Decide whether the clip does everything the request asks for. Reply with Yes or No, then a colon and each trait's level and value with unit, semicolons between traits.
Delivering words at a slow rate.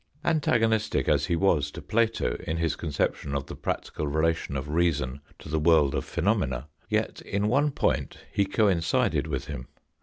No: average, 170 wpm